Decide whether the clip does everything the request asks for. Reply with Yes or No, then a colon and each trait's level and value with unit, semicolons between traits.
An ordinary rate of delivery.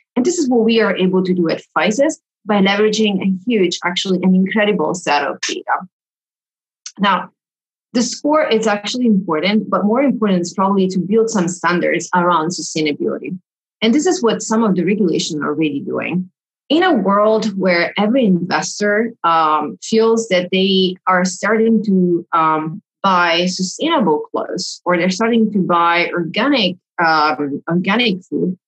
Yes: average, 155 wpm